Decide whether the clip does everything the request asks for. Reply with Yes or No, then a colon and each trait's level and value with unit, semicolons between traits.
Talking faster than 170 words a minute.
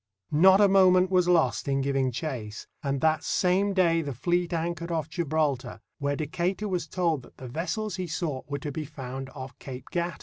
Yes: average, 195 wpm